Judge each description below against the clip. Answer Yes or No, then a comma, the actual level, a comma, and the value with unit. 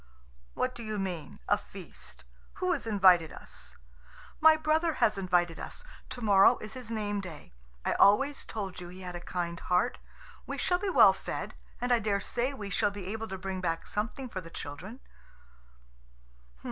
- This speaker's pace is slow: No, average, 180 wpm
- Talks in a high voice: Yes, high, 205 Hz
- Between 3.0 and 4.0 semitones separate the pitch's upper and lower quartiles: No, average, 5.2 semitones